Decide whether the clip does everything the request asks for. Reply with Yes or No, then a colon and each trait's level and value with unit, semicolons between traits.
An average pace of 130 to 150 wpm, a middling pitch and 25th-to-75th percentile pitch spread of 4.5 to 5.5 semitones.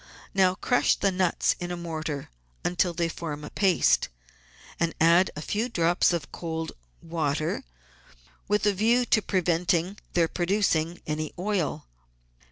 No: average, 140 wpm; medium, 175 Hz; average, 2.8 semitones